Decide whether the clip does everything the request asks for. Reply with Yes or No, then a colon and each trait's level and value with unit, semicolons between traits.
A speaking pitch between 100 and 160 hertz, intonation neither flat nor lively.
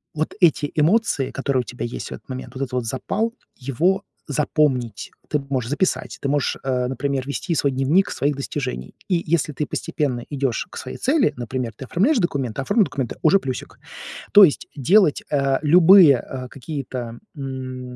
Yes: medium, 140 Hz; average, 3.9 semitones